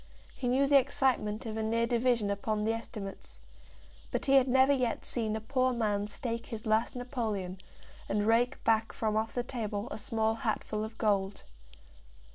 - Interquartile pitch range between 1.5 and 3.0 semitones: Yes, narrow, 2.6 semitones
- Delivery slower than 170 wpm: No, average, 175 wpm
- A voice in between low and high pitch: No, high, 225 Hz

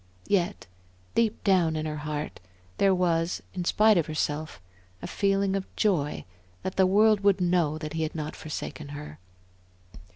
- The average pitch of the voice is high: No, medium, 175 Hz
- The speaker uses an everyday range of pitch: Yes, average, 4.1 semitones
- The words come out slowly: No, average, 160 wpm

